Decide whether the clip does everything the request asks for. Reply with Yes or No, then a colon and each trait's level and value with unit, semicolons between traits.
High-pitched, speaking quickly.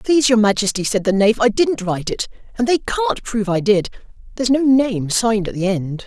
Yes: high, 220 Hz; fast, 225 wpm